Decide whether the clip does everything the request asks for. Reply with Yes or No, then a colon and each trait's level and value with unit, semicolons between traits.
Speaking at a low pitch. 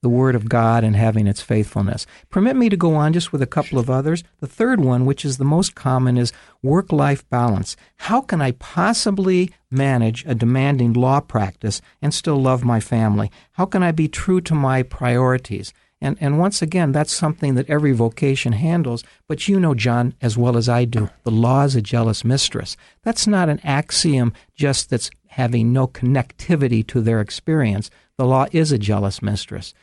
Yes: low, 130 Hz